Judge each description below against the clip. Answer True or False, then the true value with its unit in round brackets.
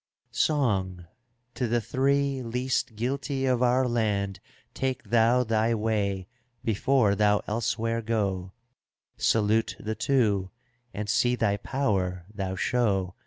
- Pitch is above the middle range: False (115 Hz)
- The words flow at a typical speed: False (120 wpm)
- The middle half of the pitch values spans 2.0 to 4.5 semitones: True (3.8 semitones)